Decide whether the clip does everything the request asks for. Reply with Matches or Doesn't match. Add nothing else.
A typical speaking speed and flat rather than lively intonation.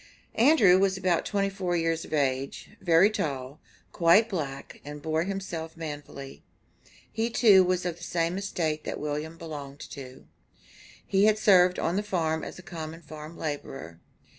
Doesn't match